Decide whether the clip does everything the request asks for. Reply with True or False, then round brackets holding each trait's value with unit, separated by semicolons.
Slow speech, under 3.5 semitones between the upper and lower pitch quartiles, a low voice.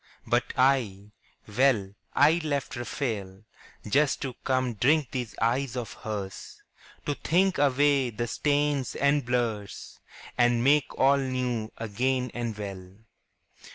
False (120 wpm; 4.0 semitones; 125 Hz)